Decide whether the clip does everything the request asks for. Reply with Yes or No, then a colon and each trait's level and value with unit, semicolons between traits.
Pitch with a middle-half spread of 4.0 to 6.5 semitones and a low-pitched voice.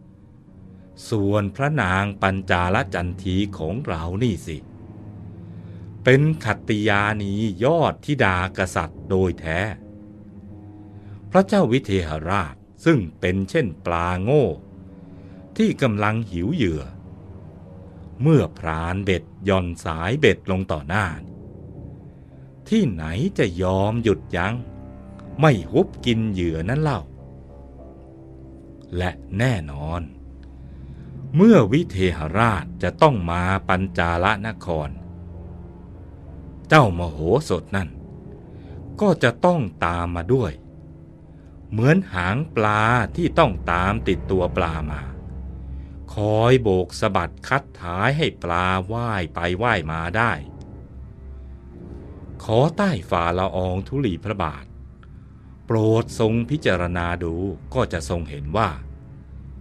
Yes: average, 4.5 semitones; very low, 95 Hz